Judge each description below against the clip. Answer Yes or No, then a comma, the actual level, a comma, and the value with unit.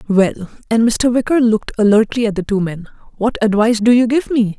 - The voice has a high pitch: Yes, high, 220 Hz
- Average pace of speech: No, fast, 210 wpm